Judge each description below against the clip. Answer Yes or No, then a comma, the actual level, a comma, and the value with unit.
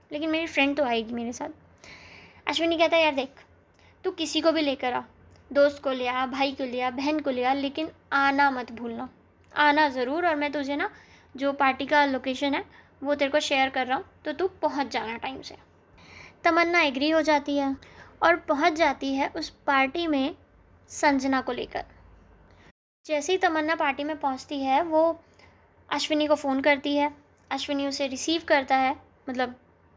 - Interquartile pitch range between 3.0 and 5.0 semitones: No, narrow, 2.5 semitones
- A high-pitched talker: Yes, very high, 285 Hz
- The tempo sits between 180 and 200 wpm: Yes, average, 185 wpm